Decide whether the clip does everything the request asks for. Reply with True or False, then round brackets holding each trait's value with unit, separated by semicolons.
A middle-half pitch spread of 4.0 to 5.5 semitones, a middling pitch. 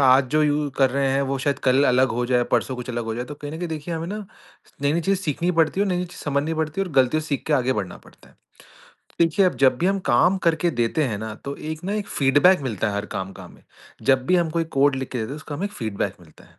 True (4.3 semitones; 145 Hz)